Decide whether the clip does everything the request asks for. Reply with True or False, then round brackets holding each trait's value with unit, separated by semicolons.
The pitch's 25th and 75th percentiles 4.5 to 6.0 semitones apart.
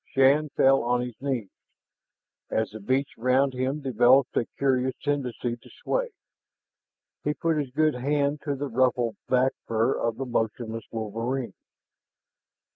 False (2.9 semitones)